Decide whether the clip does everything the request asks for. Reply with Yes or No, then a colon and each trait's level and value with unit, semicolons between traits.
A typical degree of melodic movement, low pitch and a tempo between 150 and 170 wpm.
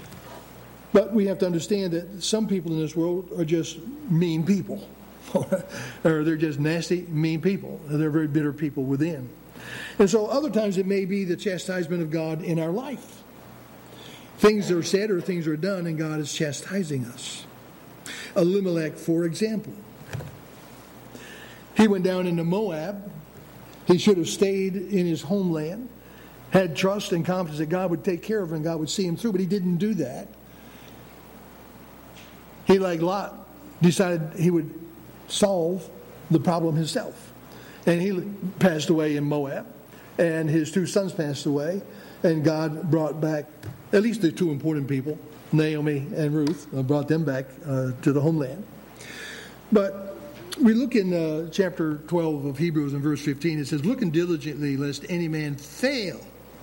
No: average, 3.6 semitones; medium, 170 Hz; average, 160 wpm